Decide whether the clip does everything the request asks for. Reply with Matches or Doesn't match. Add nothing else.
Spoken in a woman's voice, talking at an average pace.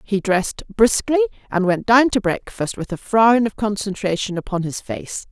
Matches